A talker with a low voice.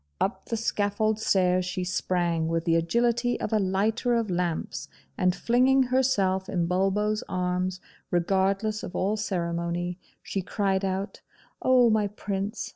No: high, 195 Hz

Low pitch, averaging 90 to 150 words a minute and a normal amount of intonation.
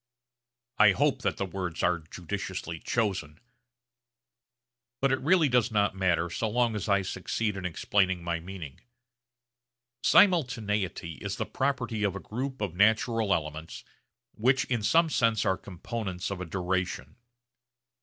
Yes: low, 100 Hz; average, 140 wpm; average, 4.5 semitones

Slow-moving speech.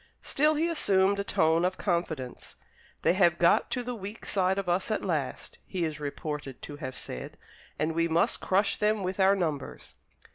No: average, 185 wpm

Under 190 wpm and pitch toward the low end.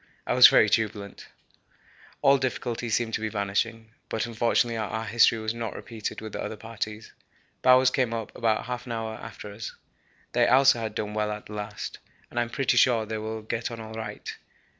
No: average, 195 wpm; low, 110 Hz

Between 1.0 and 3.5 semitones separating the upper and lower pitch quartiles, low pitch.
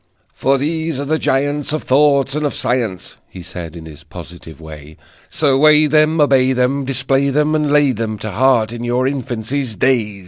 No: average, 4.9 semitones; low, 130 Hz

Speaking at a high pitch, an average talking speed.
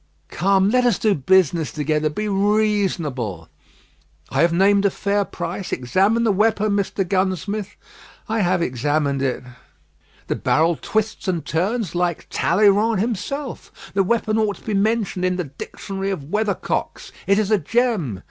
Yes: high, 195 Hz; average, 150 wpm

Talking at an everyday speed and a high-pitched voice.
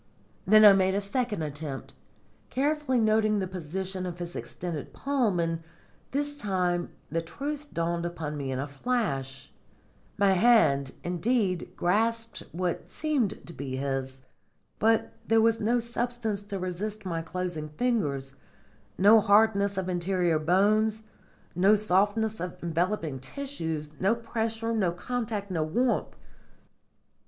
No: slow, 130 wpm; high, 195 Hz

